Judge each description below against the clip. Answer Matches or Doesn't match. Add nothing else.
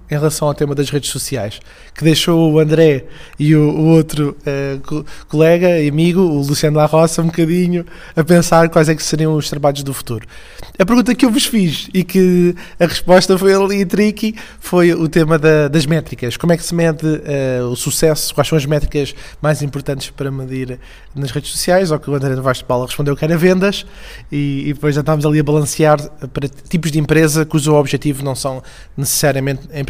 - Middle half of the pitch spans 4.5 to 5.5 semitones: Doesn't match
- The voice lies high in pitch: Doesn't match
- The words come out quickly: Matches